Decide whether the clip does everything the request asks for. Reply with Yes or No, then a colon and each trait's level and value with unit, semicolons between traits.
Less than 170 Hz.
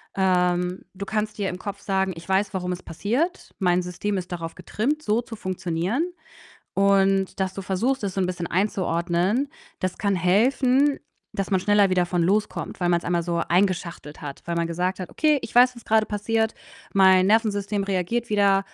No: high, 195 Hz